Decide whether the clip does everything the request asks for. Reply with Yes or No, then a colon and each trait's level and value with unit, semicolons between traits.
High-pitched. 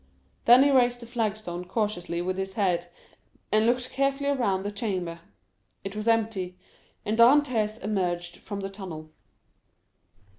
Yes: high, 210 Hz